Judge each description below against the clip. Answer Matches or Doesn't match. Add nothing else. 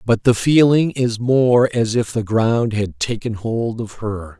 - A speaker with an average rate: Matches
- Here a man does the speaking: Matches